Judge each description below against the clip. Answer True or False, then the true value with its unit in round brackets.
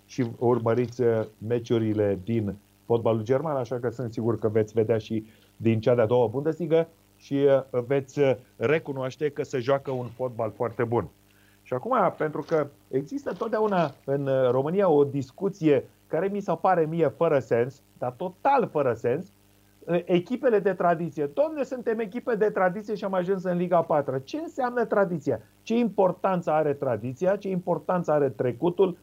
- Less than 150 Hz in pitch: True (140 Hz)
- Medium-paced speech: True (155 wpm)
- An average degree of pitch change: False (7.3 semitones)